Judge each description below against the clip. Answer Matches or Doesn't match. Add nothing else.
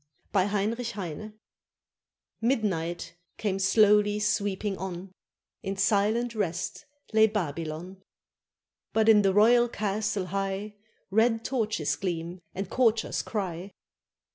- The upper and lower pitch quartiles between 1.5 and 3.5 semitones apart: Matches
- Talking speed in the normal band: Doesn't match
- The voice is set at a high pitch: Matches